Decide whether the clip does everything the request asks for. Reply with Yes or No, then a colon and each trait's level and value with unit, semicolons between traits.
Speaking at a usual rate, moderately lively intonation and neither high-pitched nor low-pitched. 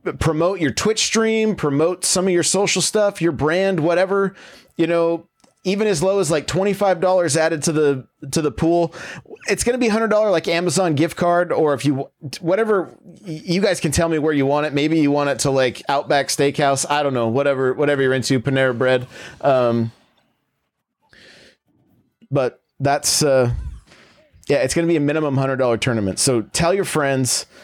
Yes: average, 175 wpm; average, 4.8 semitones; medium, 155 Hz